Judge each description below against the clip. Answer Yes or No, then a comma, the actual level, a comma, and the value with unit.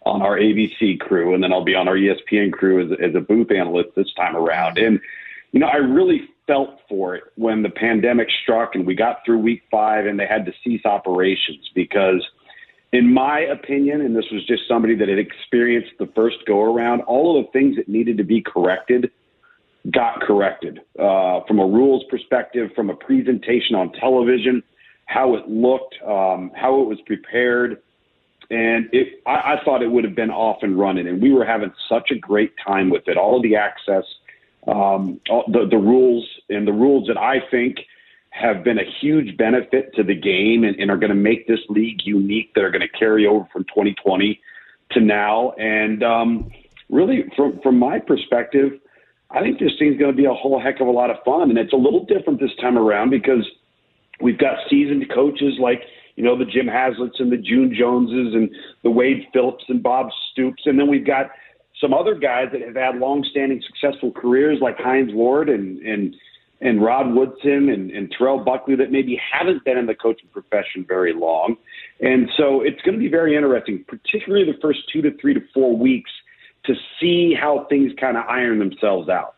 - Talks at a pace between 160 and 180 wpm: No, average, 200 wpm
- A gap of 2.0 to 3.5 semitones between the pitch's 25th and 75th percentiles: No, average, 3.9 semitones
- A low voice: Yes, low, 120 Hz